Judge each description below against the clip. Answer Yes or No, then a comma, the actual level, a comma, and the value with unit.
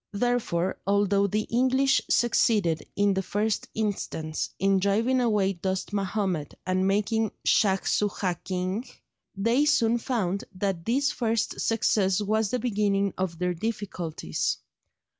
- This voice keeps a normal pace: No, slow, 125 wpm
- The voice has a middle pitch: No, high, 200 Hz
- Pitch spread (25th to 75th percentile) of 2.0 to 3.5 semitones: Yes, average, 3.1 semitones